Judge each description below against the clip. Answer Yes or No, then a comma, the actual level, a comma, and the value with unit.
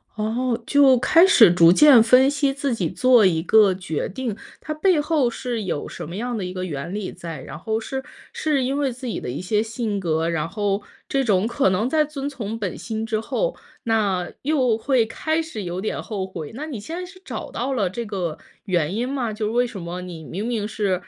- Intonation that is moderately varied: No, wide, 5.9 semitones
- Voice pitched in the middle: No, high, 220 Hz